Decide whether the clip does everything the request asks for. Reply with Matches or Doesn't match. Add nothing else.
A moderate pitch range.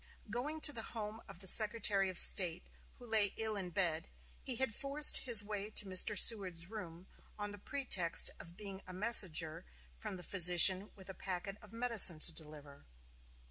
Matches